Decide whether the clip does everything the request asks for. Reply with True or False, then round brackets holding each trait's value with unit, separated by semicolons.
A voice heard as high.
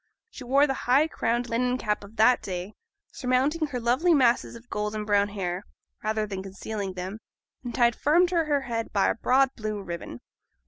True (230 Hz)